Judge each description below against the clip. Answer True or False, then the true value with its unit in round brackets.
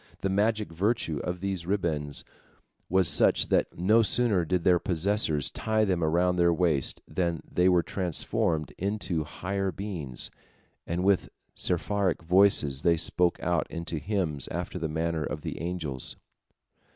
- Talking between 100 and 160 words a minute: True (145 wpm)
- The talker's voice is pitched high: False (90 Hz)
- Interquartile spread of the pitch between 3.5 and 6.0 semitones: False (3.1 semitones)